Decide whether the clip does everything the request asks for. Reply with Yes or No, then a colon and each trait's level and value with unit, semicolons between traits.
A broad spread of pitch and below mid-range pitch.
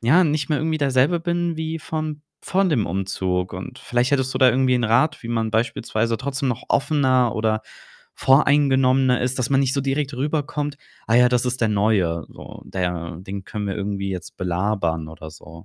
Yes: wide, 5.8 semitones; low, 125 Hz